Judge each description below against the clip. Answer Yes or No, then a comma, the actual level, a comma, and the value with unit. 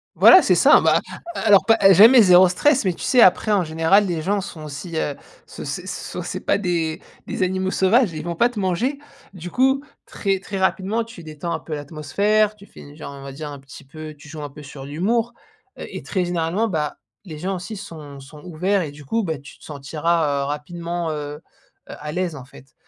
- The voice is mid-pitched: Yes, medium, 170 Hz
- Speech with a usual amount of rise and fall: Yes, average, 4.8 semitones